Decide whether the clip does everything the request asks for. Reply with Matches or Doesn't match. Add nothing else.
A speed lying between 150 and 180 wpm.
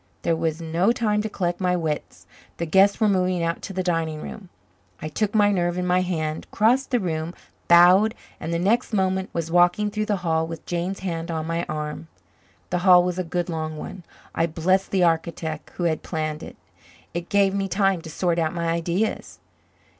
Doesn't match